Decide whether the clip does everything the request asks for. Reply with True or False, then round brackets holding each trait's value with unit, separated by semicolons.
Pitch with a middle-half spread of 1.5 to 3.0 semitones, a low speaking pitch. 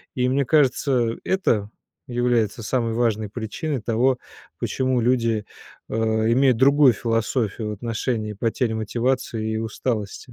True (2.7 semitones; 120 Hz)